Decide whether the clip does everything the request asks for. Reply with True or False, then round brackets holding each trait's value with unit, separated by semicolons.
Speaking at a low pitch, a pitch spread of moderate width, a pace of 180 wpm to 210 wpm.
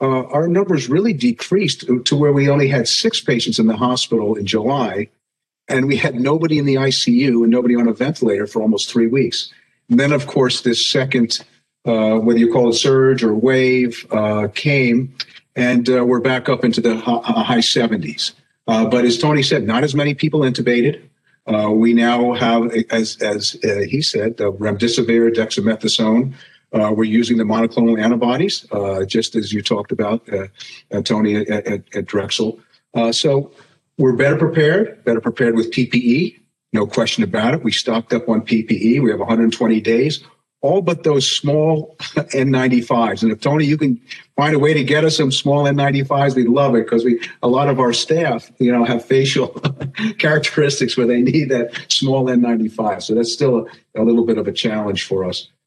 True (125 Hz; 3.5 semitones; 190 wpm)